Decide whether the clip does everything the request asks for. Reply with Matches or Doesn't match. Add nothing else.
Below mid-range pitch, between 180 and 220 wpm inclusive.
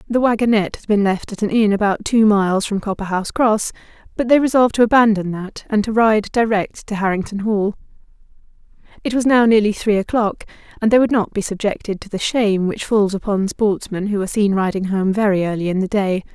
Doesn't match